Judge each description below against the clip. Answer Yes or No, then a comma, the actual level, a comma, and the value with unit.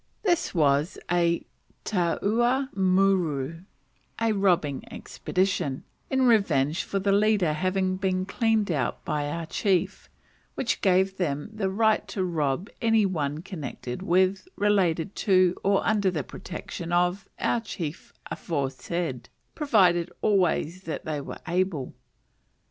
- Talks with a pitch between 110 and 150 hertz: No, medium, 185 Hz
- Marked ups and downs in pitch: No, average, 3.9 semitones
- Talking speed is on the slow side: Yes, slow, 125 wpm